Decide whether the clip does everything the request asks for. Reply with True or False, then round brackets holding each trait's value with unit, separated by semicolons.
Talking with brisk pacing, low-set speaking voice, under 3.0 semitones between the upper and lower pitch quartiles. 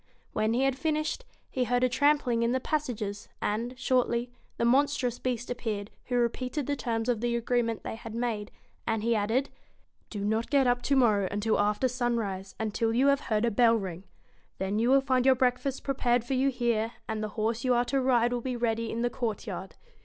False (220 wpm; 240 Hz; 2.4 semitones)